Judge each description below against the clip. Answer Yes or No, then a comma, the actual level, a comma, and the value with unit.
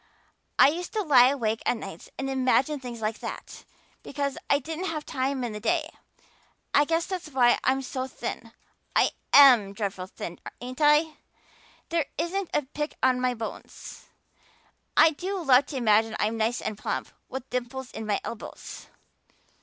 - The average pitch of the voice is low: No, very high, 265 Hz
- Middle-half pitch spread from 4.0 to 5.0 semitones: Yes, average, 4.4 semitones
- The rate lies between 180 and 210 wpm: No, average, 165 wpm